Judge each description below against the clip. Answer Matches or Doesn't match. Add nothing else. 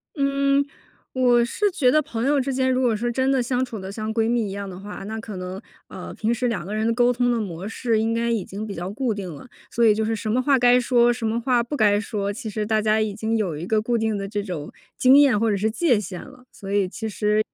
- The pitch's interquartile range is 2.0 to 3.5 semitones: Matches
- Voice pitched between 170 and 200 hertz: Doesn't match